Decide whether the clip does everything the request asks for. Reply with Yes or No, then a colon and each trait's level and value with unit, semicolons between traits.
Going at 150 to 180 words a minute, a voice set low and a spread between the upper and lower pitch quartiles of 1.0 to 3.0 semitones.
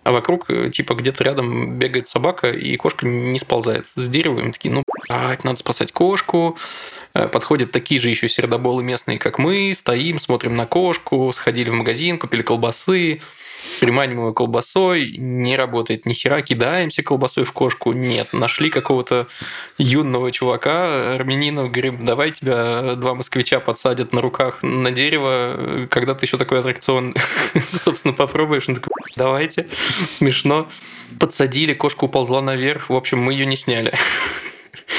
No: average, 140 wpm; low, 130 Hz; narrow, 2.6 semitones